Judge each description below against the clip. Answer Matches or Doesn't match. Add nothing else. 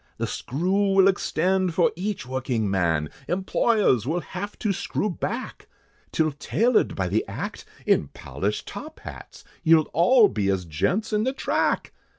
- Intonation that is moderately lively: Doesn't match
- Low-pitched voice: Doesn't match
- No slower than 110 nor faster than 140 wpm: Doesn't match